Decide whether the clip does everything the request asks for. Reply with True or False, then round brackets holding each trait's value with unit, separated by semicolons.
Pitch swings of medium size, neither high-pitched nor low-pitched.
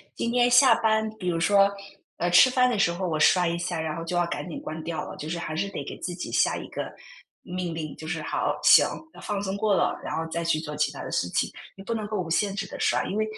True (4.0 semitones; 175 Hz)